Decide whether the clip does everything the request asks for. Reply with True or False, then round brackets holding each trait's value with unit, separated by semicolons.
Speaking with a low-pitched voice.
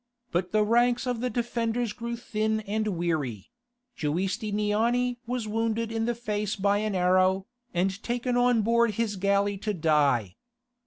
False (215 Hz)